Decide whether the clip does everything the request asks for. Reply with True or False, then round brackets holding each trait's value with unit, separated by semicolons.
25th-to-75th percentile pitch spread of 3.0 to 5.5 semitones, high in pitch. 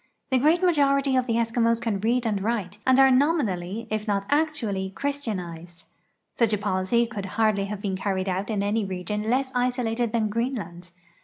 True (4.2 semitones; 225 Hz)